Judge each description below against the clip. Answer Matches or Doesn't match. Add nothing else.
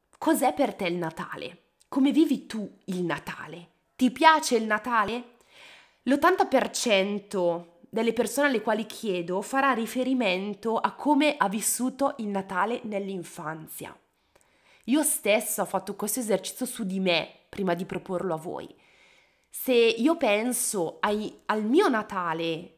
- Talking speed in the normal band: Matches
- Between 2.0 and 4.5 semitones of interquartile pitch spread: Doesn't match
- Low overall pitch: Doesn't match